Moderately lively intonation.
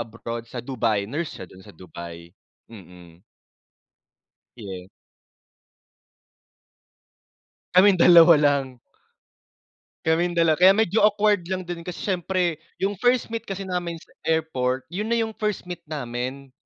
No: wide, 7.9 semitones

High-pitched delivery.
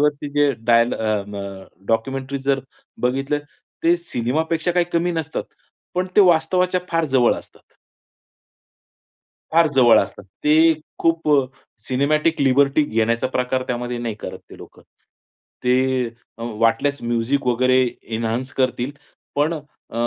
No: low, 135 Hz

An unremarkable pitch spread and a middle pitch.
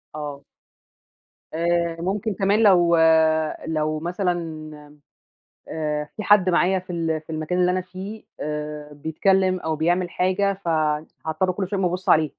Yes: average, 3.1 semitones; medium, 175 Hz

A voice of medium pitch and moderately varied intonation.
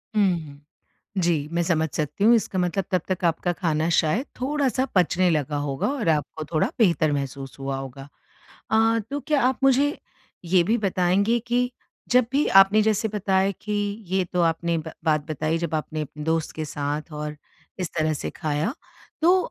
No: medium, 175 Hz; wide, 5.9 semitones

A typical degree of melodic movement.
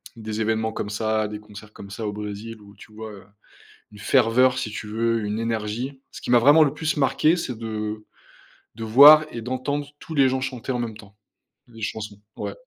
Yes: average, 3.3 semitones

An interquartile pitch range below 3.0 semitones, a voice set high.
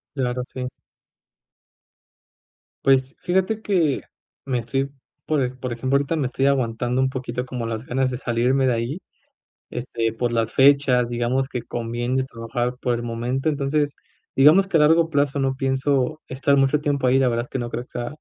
No: narrow, 2.4 semitones; low, 130 Hz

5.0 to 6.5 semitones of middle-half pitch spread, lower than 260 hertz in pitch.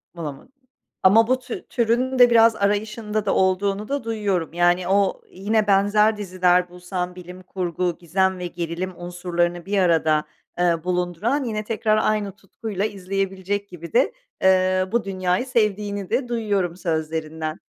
No: average, 3.2 semitones; high, 190 Hz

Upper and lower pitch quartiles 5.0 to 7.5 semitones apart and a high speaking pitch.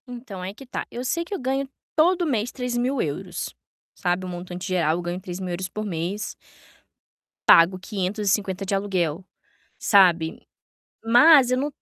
Yes: wide, 5.6 semitones; high, 195 Hz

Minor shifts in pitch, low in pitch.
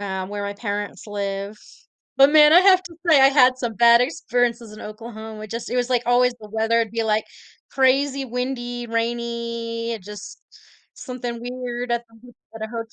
No: narrow, 2.2 semitones; high, 235 Hz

